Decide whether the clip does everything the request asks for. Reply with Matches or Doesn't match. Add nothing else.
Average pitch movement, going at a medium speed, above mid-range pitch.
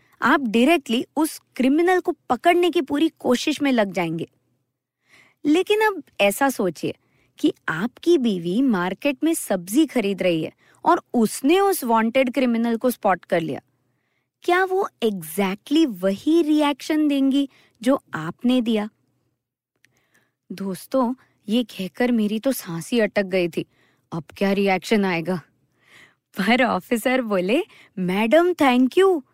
Doesn't match